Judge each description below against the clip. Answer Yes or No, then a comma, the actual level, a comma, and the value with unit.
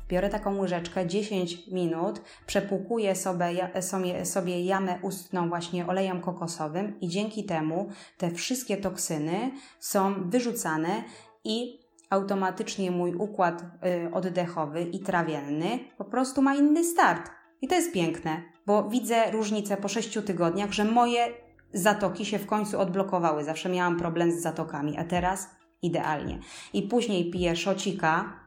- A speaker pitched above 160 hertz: Yes, high, 190 Hz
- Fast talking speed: No, average, 130 wpm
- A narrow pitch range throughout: No, average, 3.2 semitones